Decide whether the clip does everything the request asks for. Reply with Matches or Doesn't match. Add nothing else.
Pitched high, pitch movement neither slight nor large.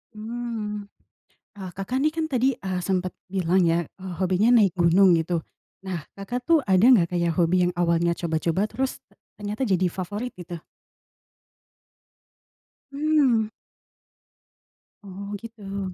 Matches